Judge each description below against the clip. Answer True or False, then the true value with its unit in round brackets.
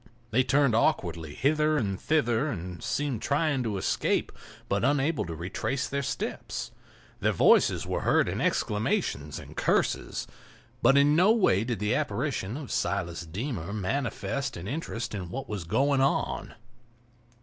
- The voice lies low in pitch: True (120 Hz)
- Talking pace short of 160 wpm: True (150 wpm)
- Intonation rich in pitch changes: True (6.7 semitones)